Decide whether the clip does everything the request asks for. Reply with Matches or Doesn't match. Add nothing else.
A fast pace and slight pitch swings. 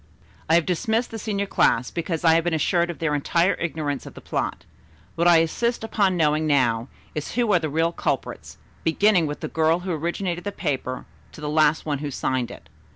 Doesn't match